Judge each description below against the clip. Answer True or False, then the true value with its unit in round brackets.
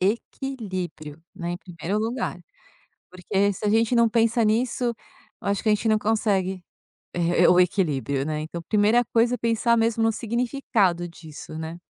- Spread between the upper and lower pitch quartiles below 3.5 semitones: False (4.7 semitones)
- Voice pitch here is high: True (205 Hz)